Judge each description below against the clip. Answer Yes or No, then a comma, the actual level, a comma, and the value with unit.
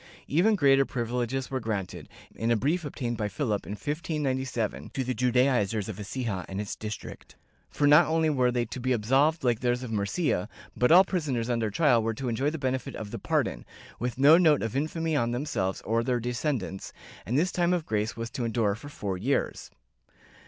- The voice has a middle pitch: No, low, 125 Hz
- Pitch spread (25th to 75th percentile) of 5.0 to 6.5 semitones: No, average, 4.5 semitones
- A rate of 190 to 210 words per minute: Yes, average, 200 wpm